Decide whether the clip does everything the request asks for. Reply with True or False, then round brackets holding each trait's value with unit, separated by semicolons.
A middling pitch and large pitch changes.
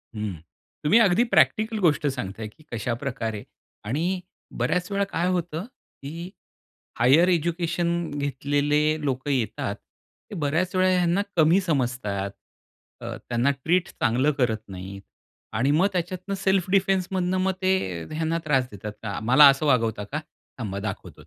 True (150 Hz; 6.7 semitones)